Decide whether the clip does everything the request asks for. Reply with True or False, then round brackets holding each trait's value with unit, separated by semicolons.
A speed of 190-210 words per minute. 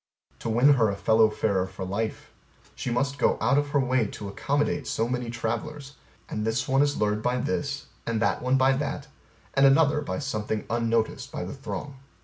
True (195 wpm)